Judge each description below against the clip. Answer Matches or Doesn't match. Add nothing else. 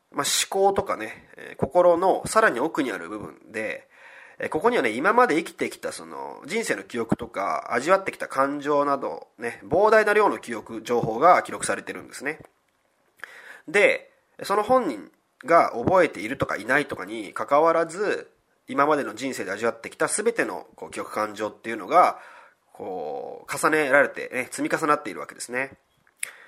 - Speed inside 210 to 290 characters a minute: Doesn't match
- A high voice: Matches